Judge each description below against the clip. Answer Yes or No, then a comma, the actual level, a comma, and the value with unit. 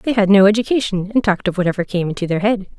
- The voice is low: No, high, 200 Hz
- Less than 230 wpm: No, fast, 260 wpm